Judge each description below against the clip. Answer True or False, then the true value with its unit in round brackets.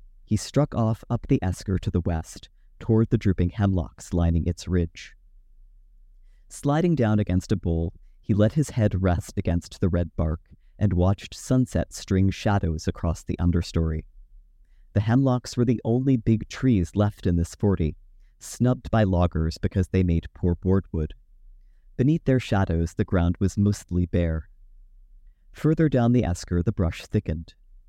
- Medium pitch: False (95 Hz)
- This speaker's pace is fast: False (155 wpm)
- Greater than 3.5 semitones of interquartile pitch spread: True (3.9 semitones)